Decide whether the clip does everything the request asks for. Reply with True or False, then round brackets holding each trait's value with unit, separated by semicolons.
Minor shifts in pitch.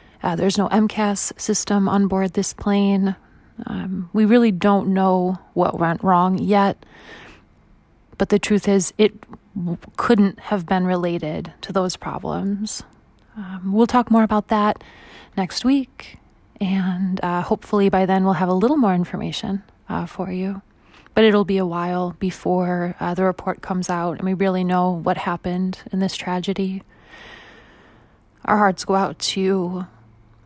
True (2.0 semitones)